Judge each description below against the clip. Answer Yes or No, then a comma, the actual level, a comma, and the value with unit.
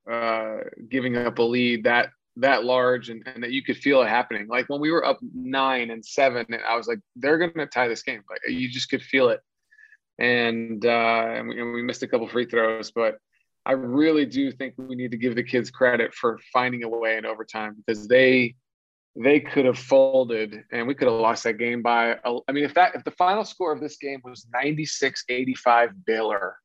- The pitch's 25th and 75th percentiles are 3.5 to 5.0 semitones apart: No, average, 3.0 semitones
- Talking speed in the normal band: No, fast, 215 wpm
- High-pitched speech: No, low, 125 Hz